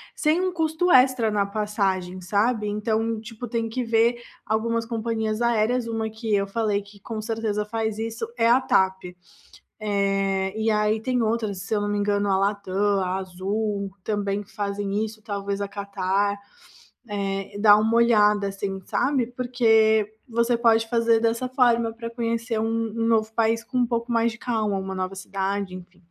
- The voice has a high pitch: Yes, high, 220 Hz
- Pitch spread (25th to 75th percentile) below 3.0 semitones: Yes, narrow, 2.4 semitones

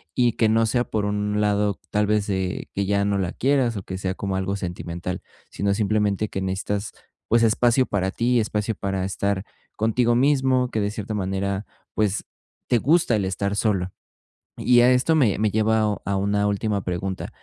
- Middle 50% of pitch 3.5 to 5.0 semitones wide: No, narrow, 2.5 semitones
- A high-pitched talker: No, low, 105 Hz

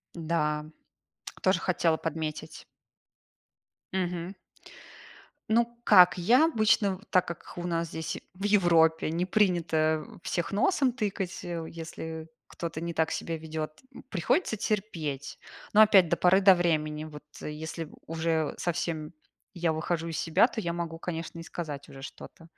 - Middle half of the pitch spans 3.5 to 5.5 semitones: No, average, 2.8 semitones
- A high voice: No, medium, 170 Hz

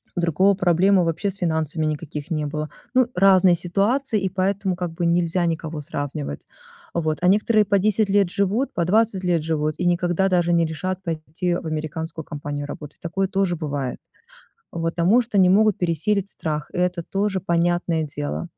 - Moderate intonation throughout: Yes, average, 3.3 semitones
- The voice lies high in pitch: No, medium, 175 Hz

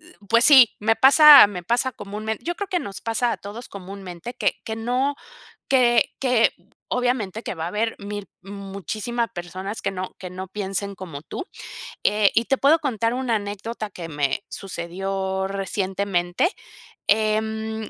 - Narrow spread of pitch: No, average, 3.7 semitones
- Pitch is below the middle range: No, high, 210 Hz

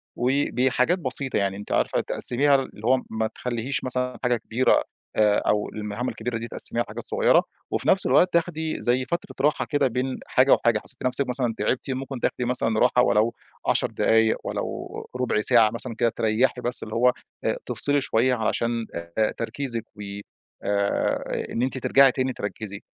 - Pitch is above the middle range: No, low, 125 Hz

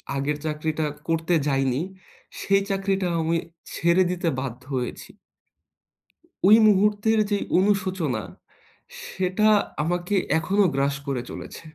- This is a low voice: No, medium, 175 Hz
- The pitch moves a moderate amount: Yes, average, 4.9 semitones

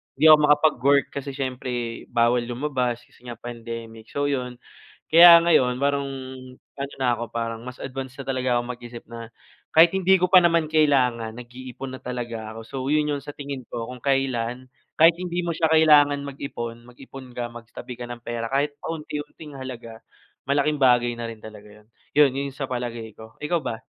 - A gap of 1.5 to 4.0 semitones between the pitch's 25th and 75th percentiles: Yes, average, 3.3 semitones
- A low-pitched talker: Yes, low, 130 Hz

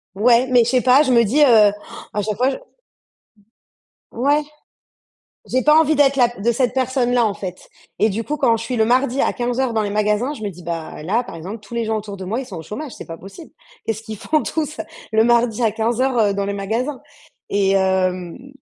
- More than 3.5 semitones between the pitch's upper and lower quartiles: Yes, average, 4.0 semitones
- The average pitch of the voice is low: No, high, 230 Hz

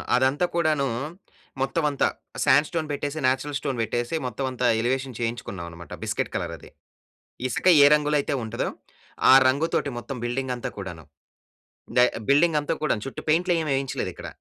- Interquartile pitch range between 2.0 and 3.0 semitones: No, average, 3.6 semitones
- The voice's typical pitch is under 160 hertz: Yes, low, 135 Hz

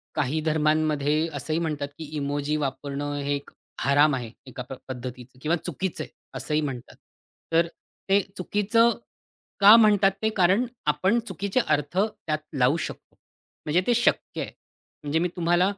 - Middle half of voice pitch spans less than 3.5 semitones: No, average, 4.6 semitones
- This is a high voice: No, medium, 155 Hz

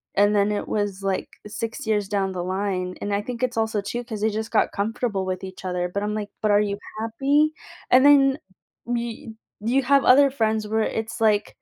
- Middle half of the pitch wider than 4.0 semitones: No, average, 2.9 semitones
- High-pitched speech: Yes, high, 215 Hz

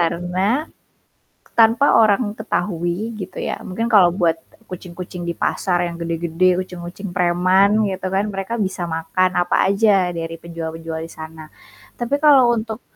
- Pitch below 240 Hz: Yes, medium, 185 Hz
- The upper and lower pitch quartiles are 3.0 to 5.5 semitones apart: Yes, average, 3.5 semitones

